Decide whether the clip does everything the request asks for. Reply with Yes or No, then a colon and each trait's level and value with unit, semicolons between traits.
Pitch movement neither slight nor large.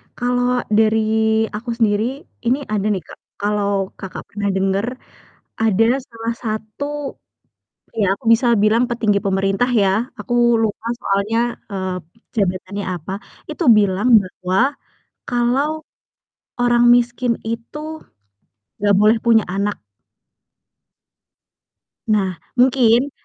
Yes: average, 3.2 semitones